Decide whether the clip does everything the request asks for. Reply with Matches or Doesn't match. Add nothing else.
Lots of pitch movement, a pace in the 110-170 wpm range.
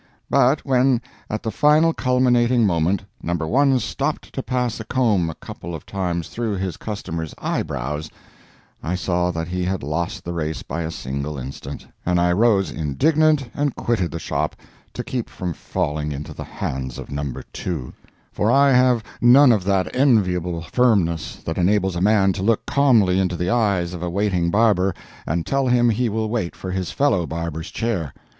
Doesn't match